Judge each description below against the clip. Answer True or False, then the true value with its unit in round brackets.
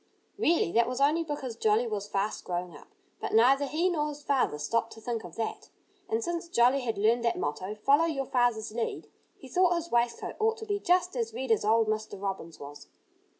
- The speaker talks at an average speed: False (210 wpm)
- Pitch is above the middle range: True (235 Hz)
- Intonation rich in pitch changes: True (5.7 semitones)